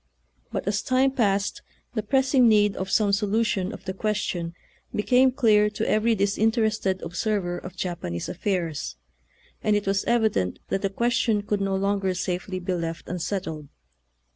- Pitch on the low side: No, high, 200 Hz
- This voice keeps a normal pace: Yes, average, 160 wpm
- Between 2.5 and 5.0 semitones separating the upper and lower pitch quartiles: Yes, average, 2.8 semitones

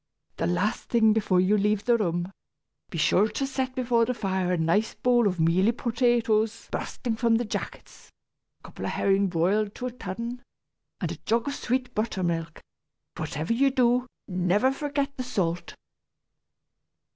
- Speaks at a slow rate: No, average, 165 wpm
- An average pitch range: Yes, average, 4.8 semitones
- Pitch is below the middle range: No, high, 220 Hz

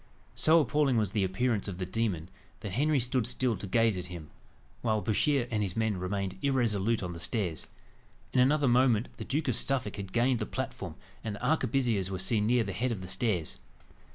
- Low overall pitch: Yes, low, 110 Hz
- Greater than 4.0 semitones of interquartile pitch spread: Yes, average, 4.8 semitones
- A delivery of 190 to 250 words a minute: Yes, fast, 205 wpm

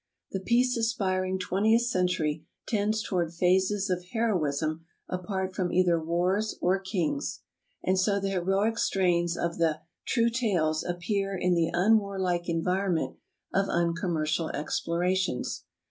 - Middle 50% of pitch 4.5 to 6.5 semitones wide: No, narrow, 2.6 semitones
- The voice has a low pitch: No, medium, 185 Hz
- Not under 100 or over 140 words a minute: Yes, slow, 135 wpm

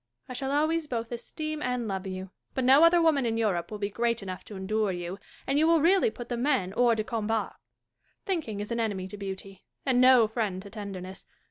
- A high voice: Yes, high, 230 Hz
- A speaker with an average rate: No, fast, 220 wpm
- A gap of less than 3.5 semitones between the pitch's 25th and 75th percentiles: No, average, 5.2 semitones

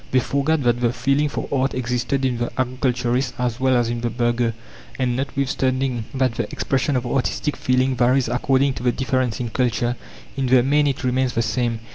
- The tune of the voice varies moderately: No, narrow, 1.8 semitones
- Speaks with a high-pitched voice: No, low, 125 Hz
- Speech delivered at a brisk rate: No, average, 195 wpm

